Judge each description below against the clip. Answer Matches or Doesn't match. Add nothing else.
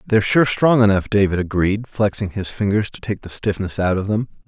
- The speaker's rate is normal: Doesn't match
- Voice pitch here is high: Doesn't match